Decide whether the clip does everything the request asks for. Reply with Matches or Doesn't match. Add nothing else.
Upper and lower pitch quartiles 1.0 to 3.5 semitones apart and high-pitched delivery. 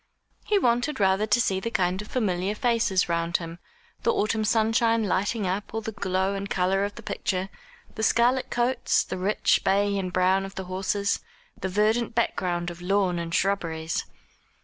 Matches